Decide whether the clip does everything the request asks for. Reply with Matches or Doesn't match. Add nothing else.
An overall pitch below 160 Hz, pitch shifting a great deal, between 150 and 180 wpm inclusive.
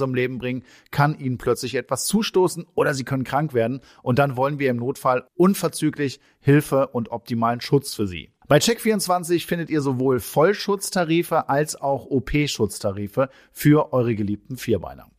Doesn't match